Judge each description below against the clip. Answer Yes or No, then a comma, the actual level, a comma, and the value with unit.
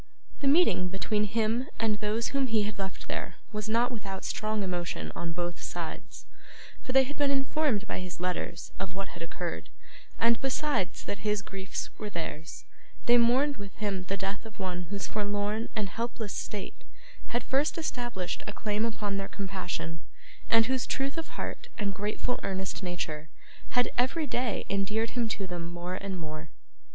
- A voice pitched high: Yes, high, 205 Hz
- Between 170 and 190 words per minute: Yes, average, 175 wpm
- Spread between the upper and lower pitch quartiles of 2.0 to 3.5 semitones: No, average, 3.9 semitones